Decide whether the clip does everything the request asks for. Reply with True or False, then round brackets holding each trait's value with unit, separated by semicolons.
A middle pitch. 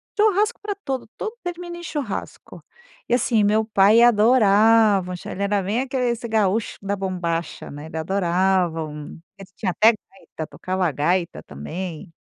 False (200 Hz)